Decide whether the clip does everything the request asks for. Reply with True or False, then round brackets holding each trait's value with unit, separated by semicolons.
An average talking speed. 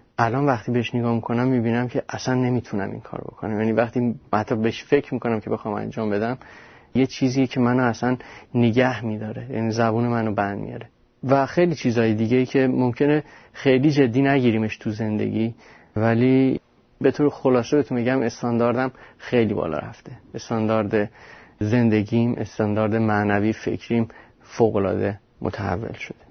True (145 wpm)